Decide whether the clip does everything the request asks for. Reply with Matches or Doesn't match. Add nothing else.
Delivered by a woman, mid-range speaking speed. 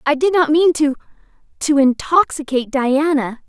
Doesn't match